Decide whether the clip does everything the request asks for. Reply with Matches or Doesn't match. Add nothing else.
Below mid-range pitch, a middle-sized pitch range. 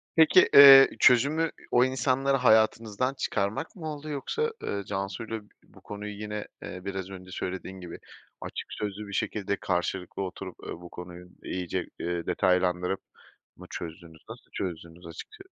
Doesn't match